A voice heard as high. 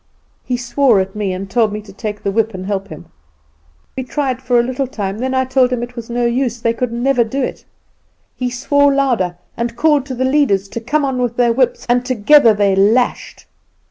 Yes: high, 240 Hz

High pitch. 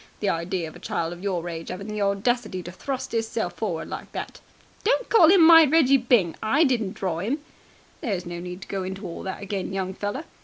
Yes: high, 200 Hz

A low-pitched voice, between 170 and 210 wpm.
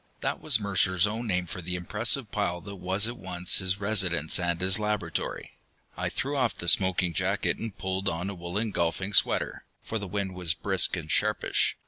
Yes: very low, 95 Hz; average, 190 wpm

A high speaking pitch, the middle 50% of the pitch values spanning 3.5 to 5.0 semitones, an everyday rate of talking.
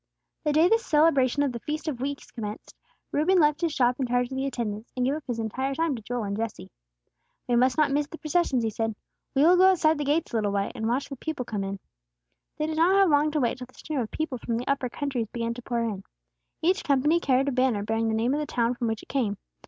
No: very high, 260 Hz; average, 4.6 semitones; fast, 265 wpm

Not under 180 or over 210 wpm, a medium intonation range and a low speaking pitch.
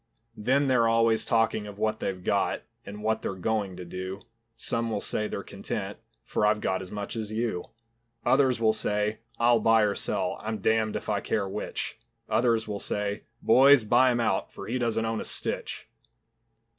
No: average, 185 wpm; narrow, 1.9 semitones; low, 110 Hz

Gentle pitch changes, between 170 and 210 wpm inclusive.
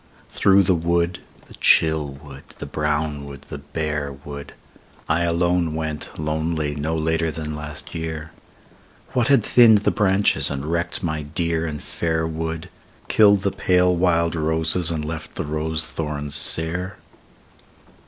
No: narrow, 2.0 semitones; average, 145 wpm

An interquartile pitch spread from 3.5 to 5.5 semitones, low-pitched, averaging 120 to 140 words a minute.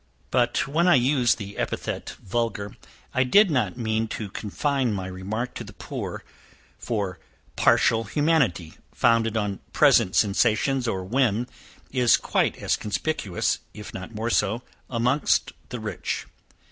Yes: average, 3.9 semitones; low, 115 Hz; slow, 135 wpm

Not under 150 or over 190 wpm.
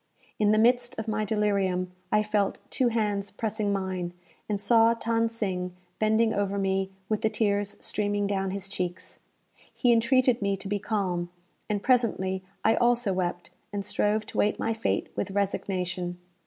Yes: average, 165 wpm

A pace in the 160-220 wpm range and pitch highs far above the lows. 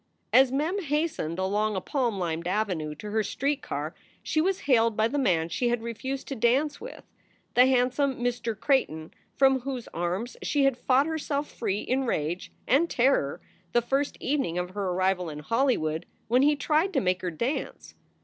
Yes: average, 180 wpm; wide, 6.7 semitones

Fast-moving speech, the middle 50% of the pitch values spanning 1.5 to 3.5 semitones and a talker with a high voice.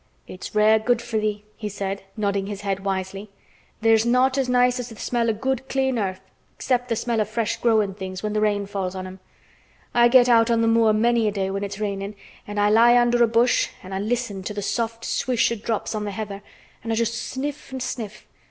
Yes: fast, 225 wpm; average, 2.9 semitones; high, 220 Hz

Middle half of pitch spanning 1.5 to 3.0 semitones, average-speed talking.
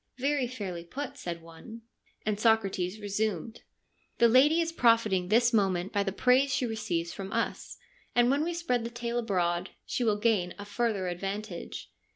No: average, 4.1 semitones; average, 180 wpm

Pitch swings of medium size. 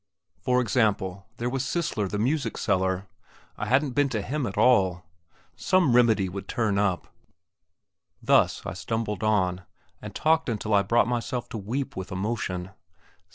Yes: average, 4.4 semitones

